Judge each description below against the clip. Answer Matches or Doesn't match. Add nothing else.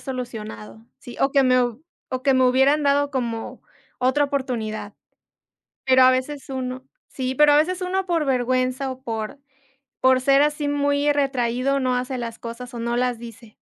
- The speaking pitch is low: Doesn't match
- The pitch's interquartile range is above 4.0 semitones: Doesn't match